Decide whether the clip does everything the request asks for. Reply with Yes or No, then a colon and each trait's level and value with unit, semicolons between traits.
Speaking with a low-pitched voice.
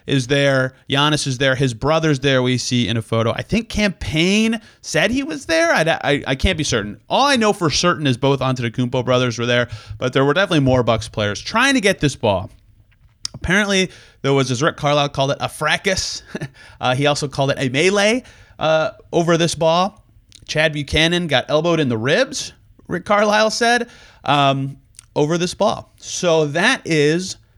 No: medium, 145 Hz